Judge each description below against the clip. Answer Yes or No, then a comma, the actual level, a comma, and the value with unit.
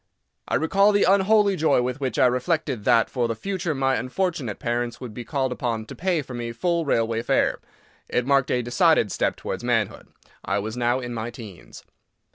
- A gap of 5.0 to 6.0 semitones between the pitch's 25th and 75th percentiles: Yes, wide, 5.5 semitones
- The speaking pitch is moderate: No, low, 125 Hz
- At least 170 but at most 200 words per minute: Yes, average, 195 wpm